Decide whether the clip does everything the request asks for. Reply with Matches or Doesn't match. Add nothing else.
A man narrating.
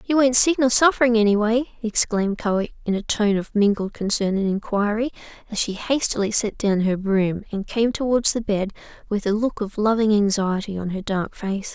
Doesn't match